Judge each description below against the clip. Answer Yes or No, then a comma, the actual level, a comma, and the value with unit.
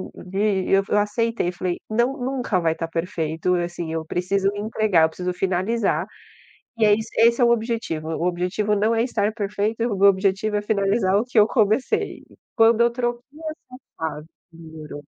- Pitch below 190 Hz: No, high, 205 Hz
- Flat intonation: No, average, 4.1 semitones